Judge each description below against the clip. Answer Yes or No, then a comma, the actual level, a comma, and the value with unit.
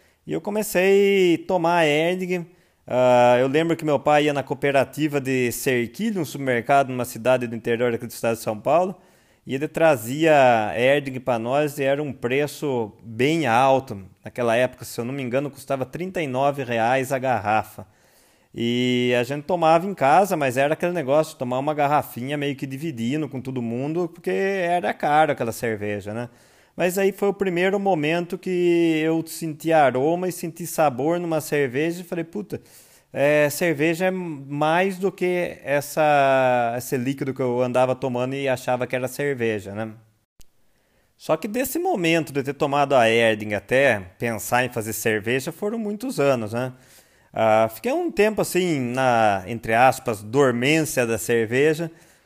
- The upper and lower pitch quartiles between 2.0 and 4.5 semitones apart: No, average, 5.1 semitones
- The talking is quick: No, average, 165 wpm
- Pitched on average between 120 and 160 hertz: Yes, medium, 140 Hz